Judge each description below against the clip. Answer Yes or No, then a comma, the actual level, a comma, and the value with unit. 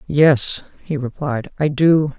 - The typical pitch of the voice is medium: Yes, medium, 145 Hz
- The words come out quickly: No, slow, 135 wpm